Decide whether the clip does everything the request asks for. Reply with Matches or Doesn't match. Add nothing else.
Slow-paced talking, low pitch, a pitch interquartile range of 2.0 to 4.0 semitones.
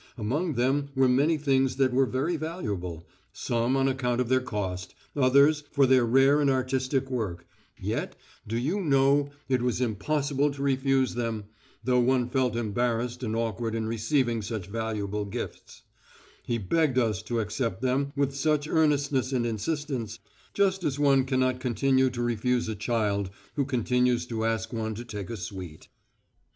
Doesn't match